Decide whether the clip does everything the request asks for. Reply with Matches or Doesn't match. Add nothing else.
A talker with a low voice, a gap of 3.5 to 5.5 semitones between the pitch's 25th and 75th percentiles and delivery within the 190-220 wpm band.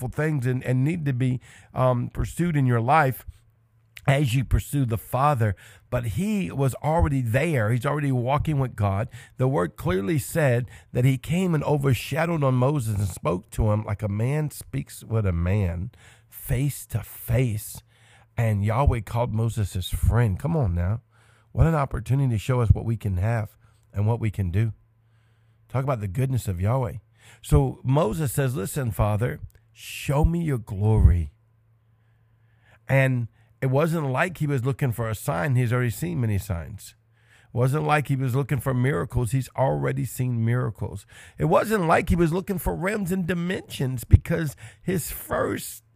Doesn't match